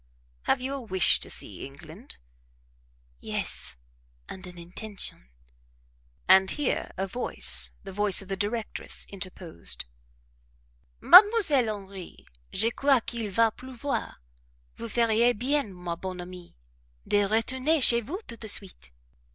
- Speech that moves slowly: Yes, slow, 125 wpm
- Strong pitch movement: No, average, 4.7 semitones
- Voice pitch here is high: Yes, high, 215 Hz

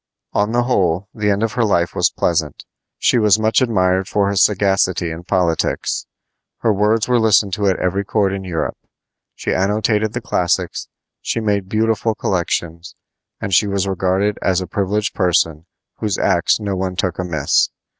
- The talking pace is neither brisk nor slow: Yes, average, 170 wpm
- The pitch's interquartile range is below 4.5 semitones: Yes, narrow, 2.6 semitones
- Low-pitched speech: Yes, low, 100 Hz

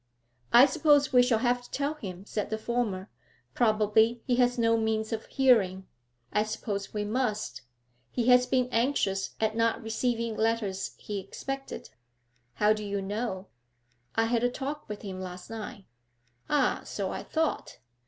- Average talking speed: Yes, average, 160 wpm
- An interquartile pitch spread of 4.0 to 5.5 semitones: No, average, 3.0 semitones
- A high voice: Yes, high, 225 Hz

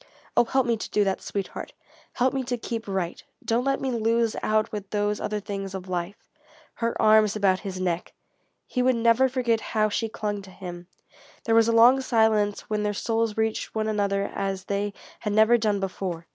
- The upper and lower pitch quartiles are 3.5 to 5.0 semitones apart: No, narrow, 2.6 semitones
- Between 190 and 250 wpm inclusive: Yes, average, 200 wpm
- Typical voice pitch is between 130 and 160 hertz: No, high, 215 Hz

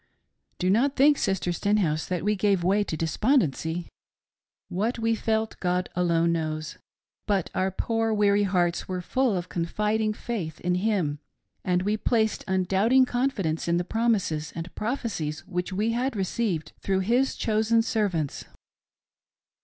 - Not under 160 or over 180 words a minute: No, average, 145 wpm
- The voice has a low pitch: No, high, 195 Hz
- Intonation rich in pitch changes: No, average, 4.3 semitones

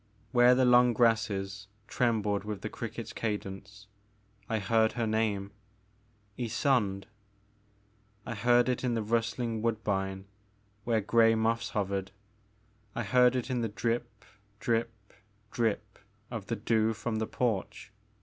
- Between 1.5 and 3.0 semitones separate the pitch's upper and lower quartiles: Yes, narrow, 2.6 semitones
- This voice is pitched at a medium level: No, low, 110 Hz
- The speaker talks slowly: Yes, slow, 130 wpm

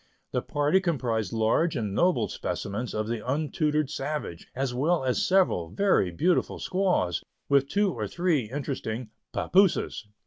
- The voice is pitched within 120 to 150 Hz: Yes, medium, 140 Hz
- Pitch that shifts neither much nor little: No, wide, 7.4 semitones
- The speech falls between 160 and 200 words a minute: No, average, 140 wpm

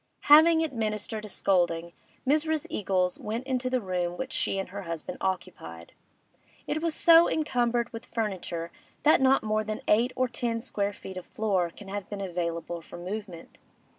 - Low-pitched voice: No, high, 210 Hz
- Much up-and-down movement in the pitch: Yes, wide, 5.7 semitones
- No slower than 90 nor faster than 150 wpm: No, average, 165 wpm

